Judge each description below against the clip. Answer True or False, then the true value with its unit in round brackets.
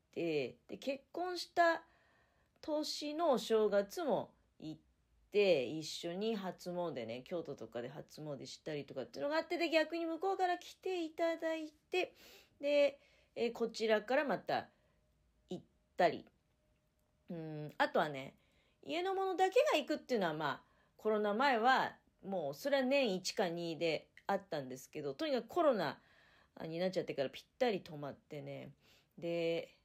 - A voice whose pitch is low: False (225 Hz)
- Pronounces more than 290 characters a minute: False (280 characters per minute)